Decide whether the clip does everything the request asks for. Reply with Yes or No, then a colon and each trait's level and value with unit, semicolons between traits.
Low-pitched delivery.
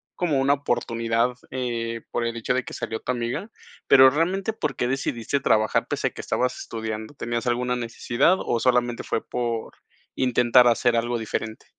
Yes: low, 120 Hz